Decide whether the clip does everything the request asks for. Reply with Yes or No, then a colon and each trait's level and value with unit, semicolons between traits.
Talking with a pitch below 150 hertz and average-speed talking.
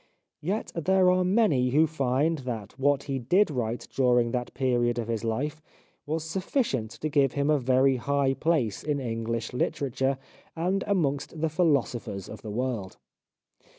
Yes: low, 135 Hz; average, 155 wpm